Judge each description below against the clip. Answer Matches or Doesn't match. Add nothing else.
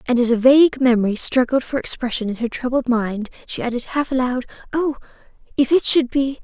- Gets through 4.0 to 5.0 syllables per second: Doesn't match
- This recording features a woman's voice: Matches